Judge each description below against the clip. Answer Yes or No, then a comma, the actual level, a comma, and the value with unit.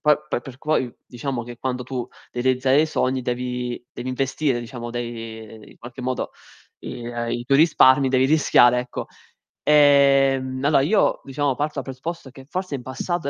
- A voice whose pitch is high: No, low, 130 Hz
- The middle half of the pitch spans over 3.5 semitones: No, narrow, 2.4 semitones